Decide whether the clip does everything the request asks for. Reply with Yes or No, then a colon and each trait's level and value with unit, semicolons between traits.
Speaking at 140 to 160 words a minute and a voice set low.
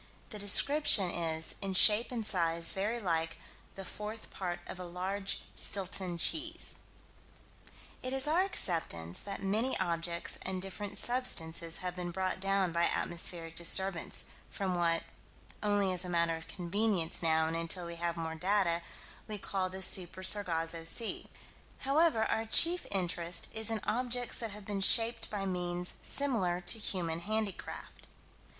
No: average, 150 wpm; medium, 185 Hz